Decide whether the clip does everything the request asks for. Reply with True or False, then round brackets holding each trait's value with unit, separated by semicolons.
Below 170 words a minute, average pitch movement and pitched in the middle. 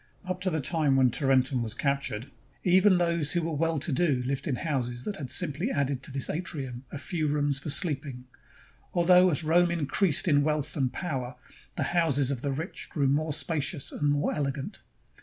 False (195 wpm; 3.8 semitones; 145 Hz)